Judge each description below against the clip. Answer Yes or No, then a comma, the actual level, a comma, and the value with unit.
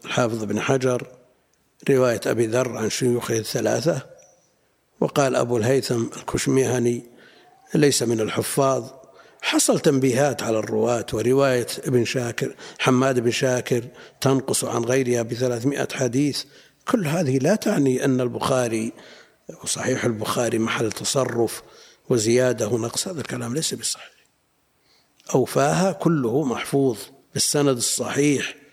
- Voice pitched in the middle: No, low, 125 Hz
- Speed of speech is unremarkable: Yes, average, 110 wpm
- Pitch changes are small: Yes, narrow, 2.3 semitones